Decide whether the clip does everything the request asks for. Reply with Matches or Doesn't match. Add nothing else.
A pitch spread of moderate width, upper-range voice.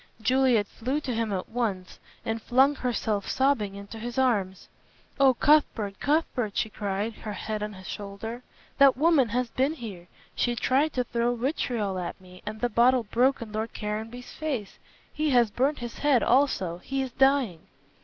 Matches